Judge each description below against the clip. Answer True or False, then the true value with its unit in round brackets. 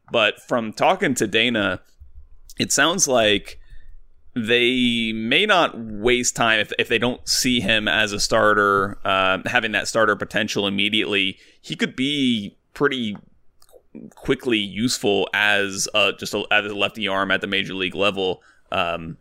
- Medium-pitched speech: False (100 Hz)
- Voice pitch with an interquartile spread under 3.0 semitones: False (4.2 semitones)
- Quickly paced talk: False (150 wpm)